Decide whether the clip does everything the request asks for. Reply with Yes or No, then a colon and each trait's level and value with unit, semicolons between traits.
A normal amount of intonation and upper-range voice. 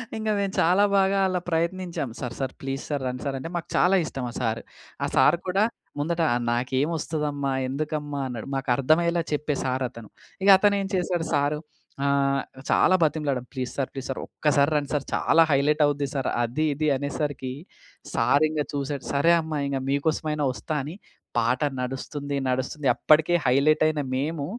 No: average, 3.0 semitones; medium, 145 Hz